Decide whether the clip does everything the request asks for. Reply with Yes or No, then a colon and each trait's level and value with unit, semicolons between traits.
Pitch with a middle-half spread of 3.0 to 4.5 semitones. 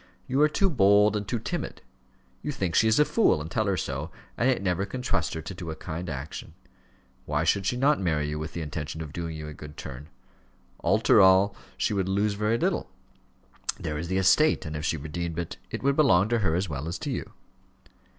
No: average, 5.2 semitones